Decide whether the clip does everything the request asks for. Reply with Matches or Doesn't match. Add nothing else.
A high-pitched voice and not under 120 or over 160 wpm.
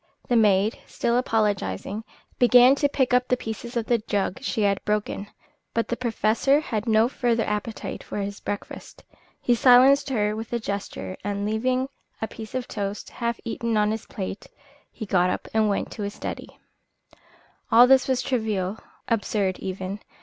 Doesn't match